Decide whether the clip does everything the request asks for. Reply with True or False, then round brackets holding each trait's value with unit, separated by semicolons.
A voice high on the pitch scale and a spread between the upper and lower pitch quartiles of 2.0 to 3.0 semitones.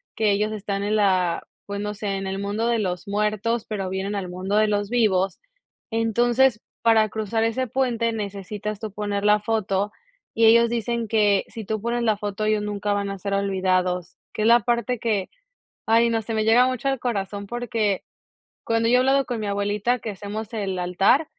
True (210 Hz; 2.4 semitones)